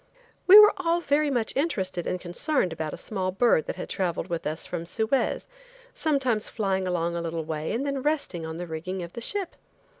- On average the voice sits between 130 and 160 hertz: No, high, 190 Hz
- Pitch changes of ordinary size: No, wide, 8.5 semitones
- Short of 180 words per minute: No, fast, 205 wpm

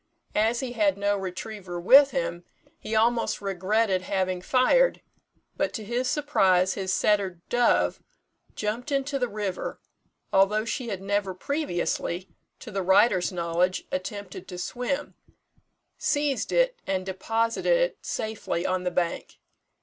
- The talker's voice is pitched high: Yes, high, 205 Hz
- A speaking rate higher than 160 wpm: No, slow, 135 wpm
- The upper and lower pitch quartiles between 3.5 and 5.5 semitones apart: Yes, average, 4.7 semitones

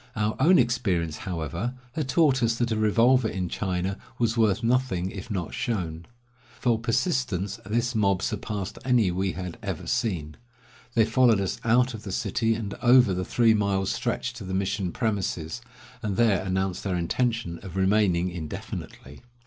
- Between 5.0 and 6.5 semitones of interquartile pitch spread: No, average, 4.2 semitones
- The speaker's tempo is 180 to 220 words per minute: No, average, 165 wpm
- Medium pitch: No, low, 105 Hz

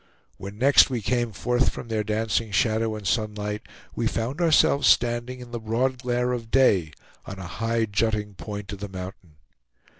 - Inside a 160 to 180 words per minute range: Yes, average, 175 wpm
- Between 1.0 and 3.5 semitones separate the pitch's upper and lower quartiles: Yes, average, 2.9 semitones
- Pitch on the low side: Yes, low, 110 Hz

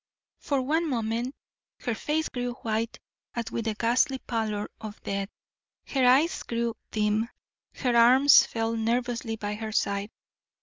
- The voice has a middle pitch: No, high, 230 Hz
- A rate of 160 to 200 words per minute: No, average, 140 wpm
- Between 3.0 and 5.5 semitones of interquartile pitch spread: No, narrow, 2.5 semitones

